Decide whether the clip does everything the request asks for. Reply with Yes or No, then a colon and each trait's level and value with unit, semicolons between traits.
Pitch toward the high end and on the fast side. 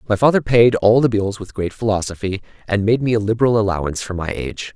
No: low, 105 Hz; fast, 225 wpm